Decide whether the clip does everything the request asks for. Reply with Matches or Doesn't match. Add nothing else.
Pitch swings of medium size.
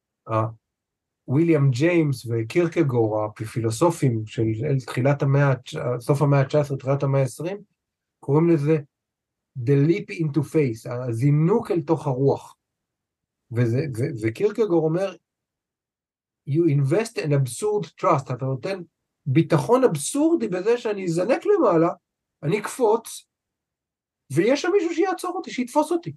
Doesn't match